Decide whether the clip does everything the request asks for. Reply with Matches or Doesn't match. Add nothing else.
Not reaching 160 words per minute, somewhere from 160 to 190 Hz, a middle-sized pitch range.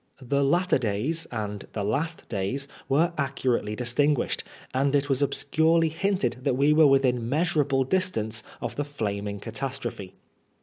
Doesn't match